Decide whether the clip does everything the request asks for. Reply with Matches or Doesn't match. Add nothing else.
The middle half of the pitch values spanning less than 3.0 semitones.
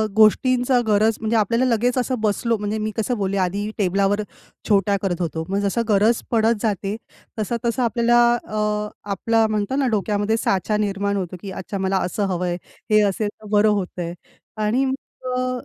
Matches